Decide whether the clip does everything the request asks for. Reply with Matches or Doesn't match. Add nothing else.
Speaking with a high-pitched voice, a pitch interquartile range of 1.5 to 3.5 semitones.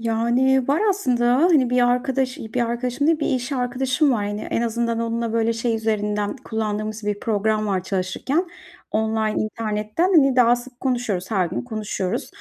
Matches